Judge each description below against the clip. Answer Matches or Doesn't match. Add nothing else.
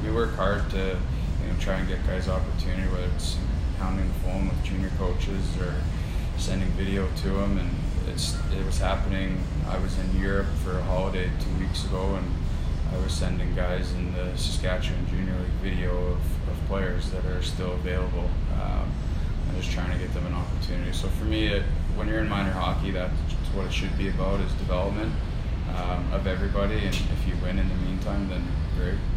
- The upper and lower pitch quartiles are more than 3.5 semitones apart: Doesn't match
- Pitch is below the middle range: Matches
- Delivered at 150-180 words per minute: Doesn't match